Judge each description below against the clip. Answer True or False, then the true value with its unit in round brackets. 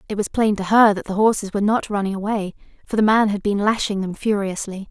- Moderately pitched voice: False (205 Hz)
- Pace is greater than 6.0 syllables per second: True (6.2 syllables/s)